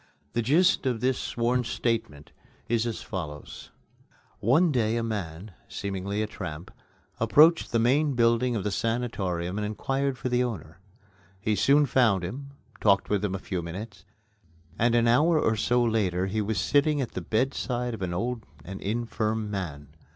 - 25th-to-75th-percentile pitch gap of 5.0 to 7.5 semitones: No, average, 4.1 semitones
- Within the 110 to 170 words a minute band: Yes, average, 165 wpm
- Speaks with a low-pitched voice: Yes, low, 115 Hz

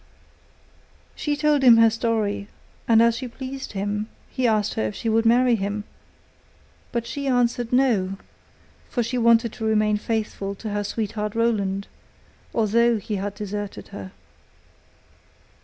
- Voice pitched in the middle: No, high, 225 Hz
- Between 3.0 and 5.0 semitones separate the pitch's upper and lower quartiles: No, narrow, 2.4 semitones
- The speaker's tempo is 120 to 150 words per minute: Yes, average, 140 wpm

